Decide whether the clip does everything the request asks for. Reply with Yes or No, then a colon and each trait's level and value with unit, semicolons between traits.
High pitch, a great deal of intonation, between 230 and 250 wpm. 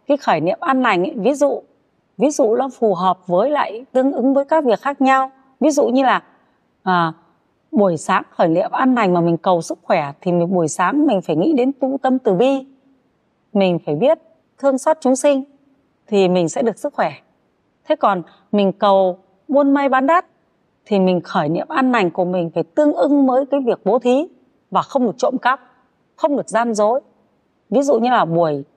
No: very high, 255 Hz; wide, 6.7 semitones; average, 210 wpm